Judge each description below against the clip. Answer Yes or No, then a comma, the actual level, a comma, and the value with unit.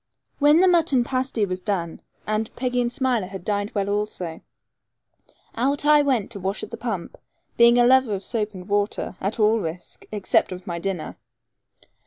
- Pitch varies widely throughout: No, average, 4.5 semitones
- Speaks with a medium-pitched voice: No, high, 215 Hz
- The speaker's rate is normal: Yes, average, 180 wpm